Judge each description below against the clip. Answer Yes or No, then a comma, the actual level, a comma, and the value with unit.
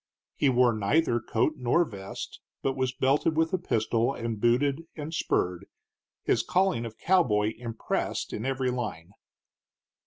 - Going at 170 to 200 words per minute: No, average, 145 wpm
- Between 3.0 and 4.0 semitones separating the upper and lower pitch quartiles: No, average, 4.7 semitones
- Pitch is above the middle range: No, low, 125 Hz